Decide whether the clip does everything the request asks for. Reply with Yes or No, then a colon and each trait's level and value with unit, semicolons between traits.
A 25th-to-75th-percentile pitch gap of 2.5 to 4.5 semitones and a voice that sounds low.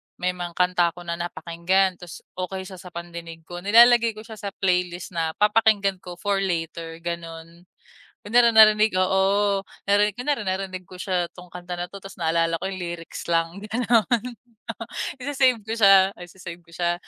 No: average, 2.9 semitones; medium, 185 Hz